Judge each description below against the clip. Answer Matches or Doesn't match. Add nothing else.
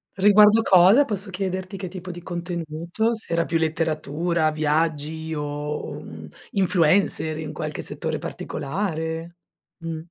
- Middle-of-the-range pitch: Matches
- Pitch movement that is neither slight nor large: Matches